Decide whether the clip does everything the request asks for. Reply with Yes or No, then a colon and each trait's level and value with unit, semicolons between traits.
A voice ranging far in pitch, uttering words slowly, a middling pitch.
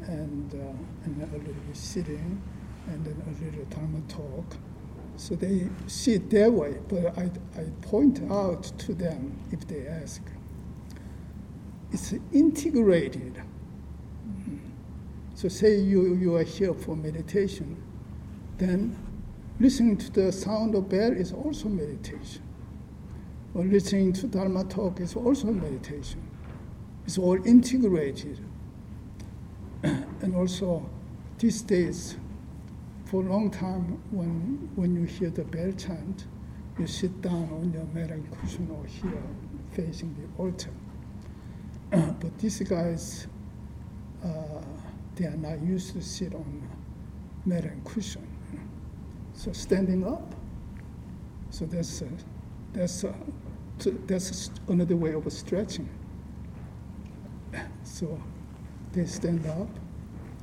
No: average, 3.7 semitones; slow, 115 wpm; medium, 180 Hz